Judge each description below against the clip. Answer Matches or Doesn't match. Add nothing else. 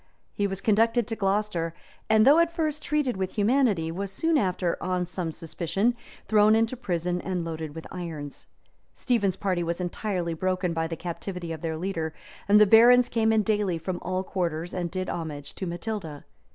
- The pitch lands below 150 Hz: Doesn't match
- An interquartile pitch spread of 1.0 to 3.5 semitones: Doesn't match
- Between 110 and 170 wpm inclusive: Doesn't match